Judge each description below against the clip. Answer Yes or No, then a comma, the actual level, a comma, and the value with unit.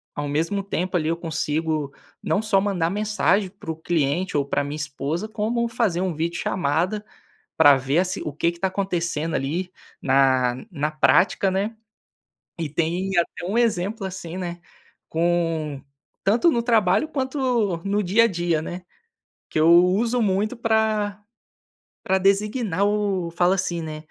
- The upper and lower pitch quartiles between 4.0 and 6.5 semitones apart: Yes, average, 4.3 semitones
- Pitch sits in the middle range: Yes, medium, 180 Hz